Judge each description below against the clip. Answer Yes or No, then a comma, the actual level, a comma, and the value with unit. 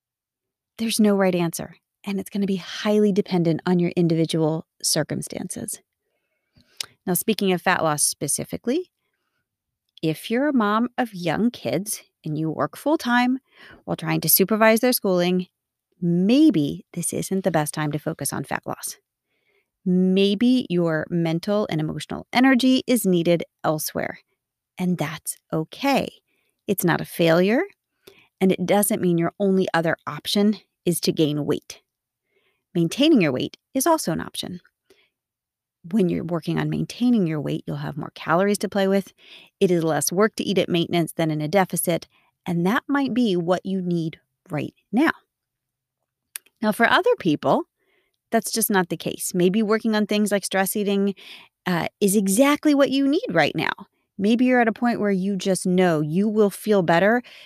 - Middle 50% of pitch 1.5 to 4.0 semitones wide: No, average, 4.8 semitones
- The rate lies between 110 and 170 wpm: Yes, average, 165 wpm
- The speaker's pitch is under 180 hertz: No, high, 195 Hz